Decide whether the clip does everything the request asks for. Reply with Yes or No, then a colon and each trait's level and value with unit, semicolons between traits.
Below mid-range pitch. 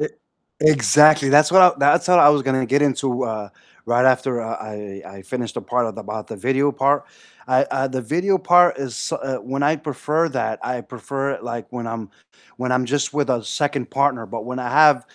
Yes: low, 130 Hz